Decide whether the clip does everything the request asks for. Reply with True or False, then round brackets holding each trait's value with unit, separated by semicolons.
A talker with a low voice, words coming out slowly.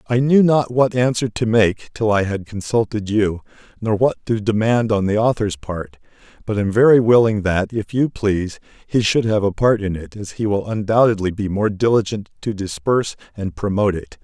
False (110 Hz; 200 wpm)